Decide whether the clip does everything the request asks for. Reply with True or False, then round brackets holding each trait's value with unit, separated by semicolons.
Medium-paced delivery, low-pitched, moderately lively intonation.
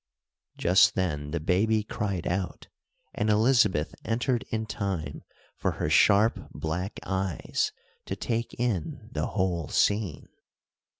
False (120 wpm; 100 Hz; 4.0 semitones)